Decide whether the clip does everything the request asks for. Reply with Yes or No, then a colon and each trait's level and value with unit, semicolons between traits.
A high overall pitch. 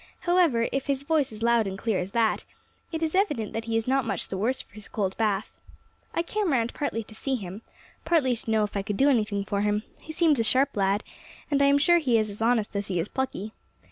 Yes: high, 230 Hz